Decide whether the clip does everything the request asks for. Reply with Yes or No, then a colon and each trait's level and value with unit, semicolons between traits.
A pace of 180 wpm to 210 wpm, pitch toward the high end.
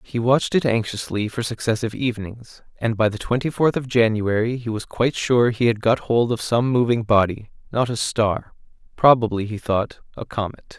No: average, 190 wpm; low, 115 Hz